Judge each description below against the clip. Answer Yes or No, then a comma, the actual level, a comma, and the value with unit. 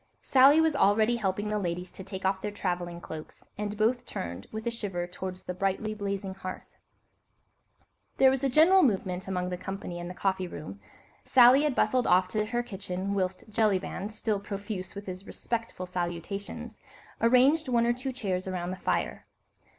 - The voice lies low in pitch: No, high, 200 Hz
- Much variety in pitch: No, average, 4.1 semitones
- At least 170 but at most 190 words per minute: Yes, average, 175 wpm